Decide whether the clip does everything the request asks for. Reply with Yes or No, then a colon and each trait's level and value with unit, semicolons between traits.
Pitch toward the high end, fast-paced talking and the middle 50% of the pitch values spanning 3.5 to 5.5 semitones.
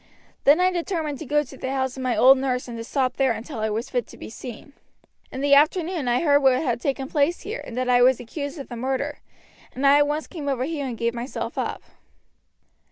No: very high, 270 Hz; fast, 240 wpm; average, 2.8 semitones